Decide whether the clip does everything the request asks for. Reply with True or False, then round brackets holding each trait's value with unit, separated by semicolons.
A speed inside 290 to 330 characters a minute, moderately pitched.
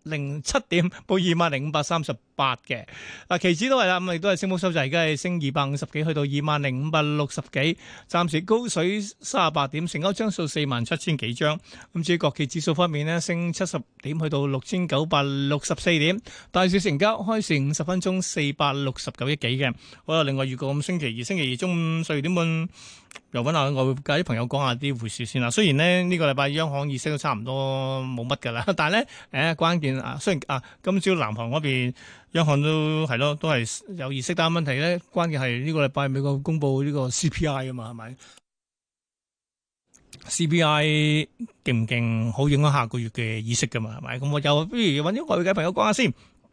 True (315 characters per minute; 150 Hz)